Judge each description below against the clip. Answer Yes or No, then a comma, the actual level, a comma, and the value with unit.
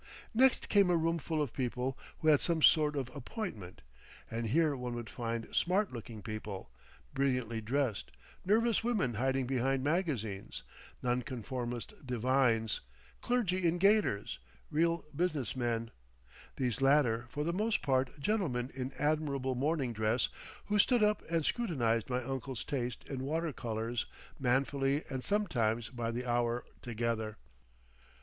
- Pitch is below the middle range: Yes, low, 130 Hz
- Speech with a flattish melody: No, average, 5.3 semitones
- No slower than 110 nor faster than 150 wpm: Yes, average, 140 wpm